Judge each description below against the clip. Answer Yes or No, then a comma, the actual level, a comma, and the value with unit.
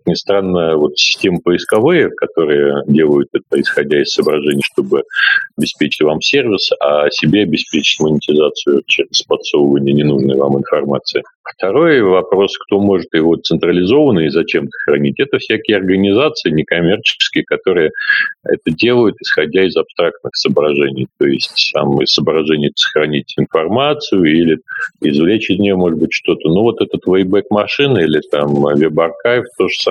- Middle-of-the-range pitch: No, very low, 95 Hz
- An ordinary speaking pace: Yes, average, 135 wpm